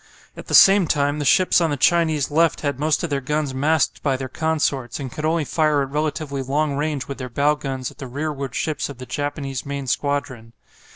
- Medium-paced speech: No, fast, 220 wpm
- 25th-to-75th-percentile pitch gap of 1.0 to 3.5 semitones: Yes, narrow, 2.4 semitones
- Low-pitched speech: No, medium, 145 Hz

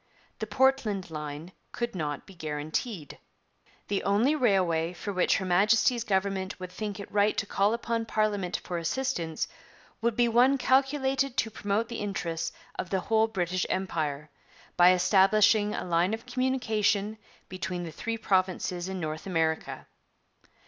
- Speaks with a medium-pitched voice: No, high, 200 Hz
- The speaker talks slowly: No, average, 150 wpm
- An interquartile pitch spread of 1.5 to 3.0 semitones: No, average, 4.3 semitones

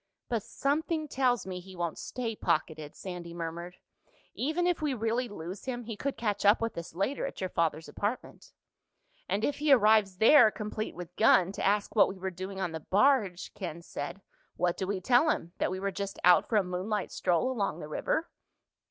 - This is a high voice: Yes, high, 200 Hz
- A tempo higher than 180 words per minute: Yes, average, 200 wpm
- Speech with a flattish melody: No, average, 5.2 semitones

